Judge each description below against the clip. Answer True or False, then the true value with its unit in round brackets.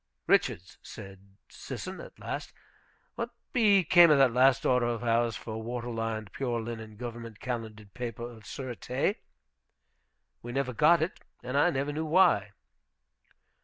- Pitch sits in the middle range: False (120 Hz)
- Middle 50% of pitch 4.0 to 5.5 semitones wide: False (3.6 semitones)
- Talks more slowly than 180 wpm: True (140 wpm)